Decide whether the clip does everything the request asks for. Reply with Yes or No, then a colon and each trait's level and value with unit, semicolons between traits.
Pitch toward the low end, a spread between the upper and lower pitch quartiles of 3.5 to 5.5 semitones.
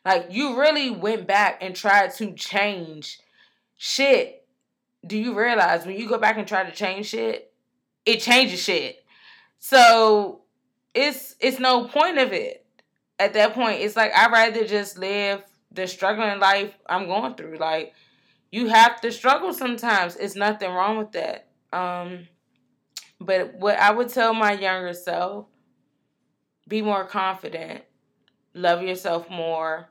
No: high, 210 Hz; average, 4.5 semitones